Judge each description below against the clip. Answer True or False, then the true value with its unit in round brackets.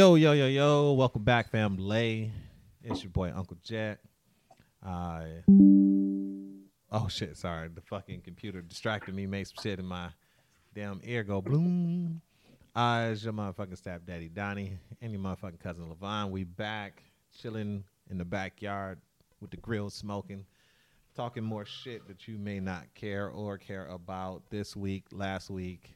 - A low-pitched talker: True (100 Hz)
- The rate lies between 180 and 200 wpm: False (155 wpm)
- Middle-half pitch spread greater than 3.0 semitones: False (2.7 semitones)